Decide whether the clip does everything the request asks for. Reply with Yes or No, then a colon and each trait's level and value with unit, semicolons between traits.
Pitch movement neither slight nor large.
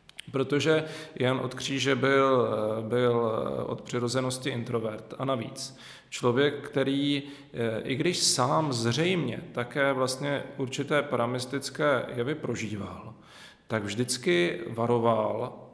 Yes: average, 3.0 semitones